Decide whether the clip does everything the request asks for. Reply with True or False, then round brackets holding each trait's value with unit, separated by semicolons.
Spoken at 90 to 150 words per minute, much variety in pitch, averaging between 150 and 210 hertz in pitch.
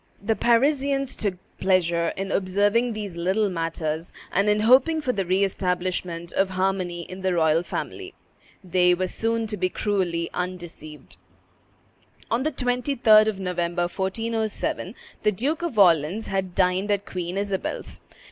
False (145 wpm; 3.8 semitones; 190 Hz)